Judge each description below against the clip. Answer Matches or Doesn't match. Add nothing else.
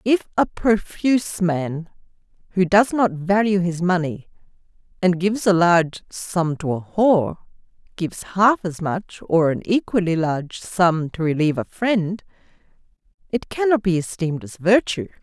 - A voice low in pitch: Doesn't match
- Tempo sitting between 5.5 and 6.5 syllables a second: Doesn't match